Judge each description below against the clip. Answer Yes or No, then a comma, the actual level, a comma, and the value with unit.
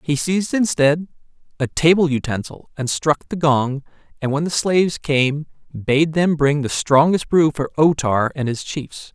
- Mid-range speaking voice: Yes, medium, 150 Hz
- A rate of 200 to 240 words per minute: No, average, 175 wpm